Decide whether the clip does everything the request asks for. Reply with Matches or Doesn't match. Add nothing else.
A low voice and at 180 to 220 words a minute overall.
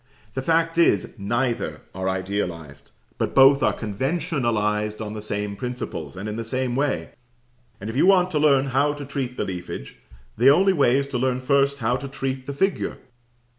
Matches